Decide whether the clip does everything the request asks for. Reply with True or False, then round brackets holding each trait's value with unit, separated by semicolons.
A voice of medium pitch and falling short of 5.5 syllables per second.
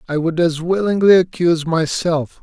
True (165 Hz; 4.9 syllables/s)